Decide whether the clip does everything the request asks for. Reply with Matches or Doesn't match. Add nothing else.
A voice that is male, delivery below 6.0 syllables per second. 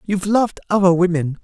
Doesn't match